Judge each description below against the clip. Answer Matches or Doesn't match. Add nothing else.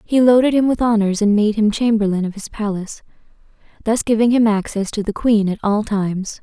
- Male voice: Doesn't match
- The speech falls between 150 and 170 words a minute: Doesn't match